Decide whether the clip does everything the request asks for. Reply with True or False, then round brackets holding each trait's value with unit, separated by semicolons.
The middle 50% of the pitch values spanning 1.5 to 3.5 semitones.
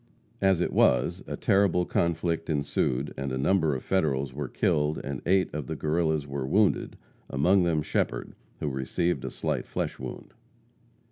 False (4.3 semitones)